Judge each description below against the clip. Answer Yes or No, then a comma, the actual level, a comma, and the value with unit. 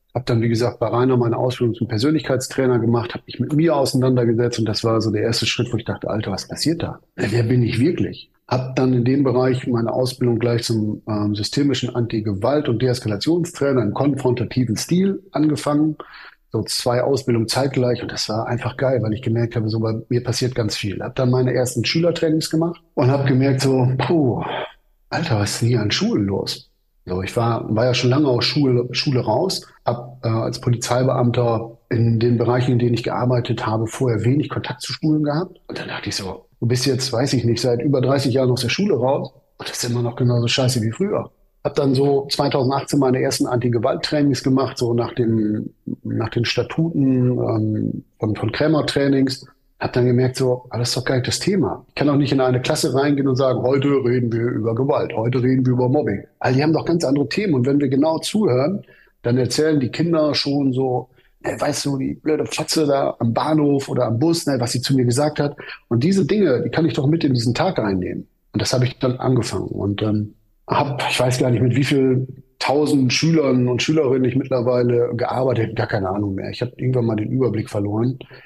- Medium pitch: No, low, 125 Hz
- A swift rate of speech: Yes, fast, 215 wpm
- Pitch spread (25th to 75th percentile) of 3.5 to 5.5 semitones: No, average, 2.8 semitones